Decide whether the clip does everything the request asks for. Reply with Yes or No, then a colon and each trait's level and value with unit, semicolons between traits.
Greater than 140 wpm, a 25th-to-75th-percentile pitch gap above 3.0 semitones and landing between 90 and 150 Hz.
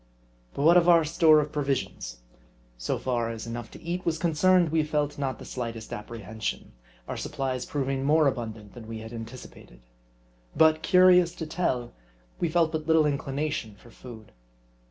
Yes: average, 165 wpm; wide, 5.5 semitones; medium, 140 Hz